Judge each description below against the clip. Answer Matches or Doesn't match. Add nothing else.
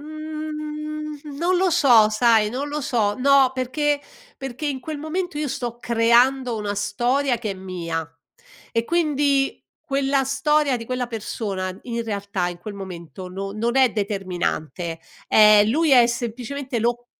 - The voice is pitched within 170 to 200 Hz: Doesn't match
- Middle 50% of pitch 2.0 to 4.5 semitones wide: Doesn't match